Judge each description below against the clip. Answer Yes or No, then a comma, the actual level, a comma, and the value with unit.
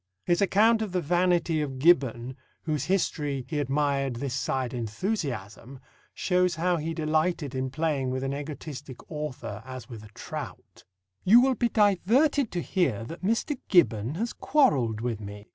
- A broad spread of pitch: Yes, wide, 5.8 semitones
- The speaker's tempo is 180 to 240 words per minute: No, average, 160 wpm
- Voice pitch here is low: No, medium, 150 Hz